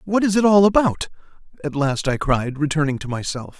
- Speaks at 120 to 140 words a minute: No, average, 200 wpm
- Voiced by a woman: No, male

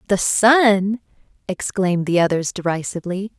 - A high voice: Yes, high, 195 Hz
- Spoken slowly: Yes, slow, 105 wpm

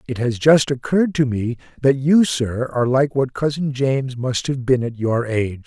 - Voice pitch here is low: Yes, low, 130 Hz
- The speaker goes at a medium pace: No, fast, 210 wpm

